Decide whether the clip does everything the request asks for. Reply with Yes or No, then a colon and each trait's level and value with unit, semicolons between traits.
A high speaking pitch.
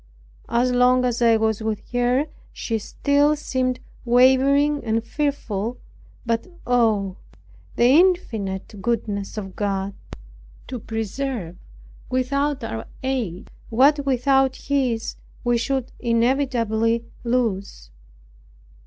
Yes: high, 240 Hz